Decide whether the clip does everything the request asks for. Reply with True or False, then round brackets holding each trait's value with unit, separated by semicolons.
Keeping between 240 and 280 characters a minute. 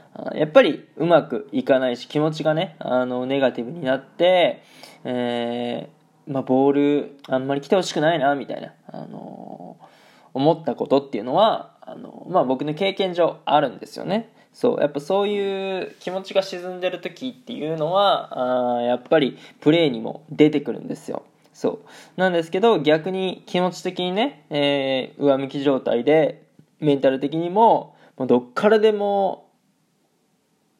False (315 characters per minute)